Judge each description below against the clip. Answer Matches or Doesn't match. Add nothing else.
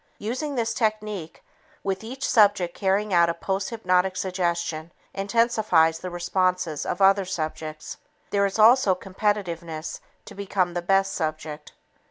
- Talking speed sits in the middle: Doesn't match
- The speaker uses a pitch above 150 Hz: Matches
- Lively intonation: Doesn't match